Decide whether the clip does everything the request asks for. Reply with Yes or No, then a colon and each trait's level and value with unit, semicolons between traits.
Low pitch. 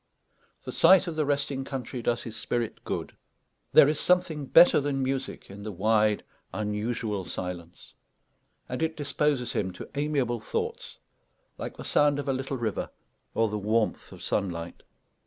Yes: low, 125 Hz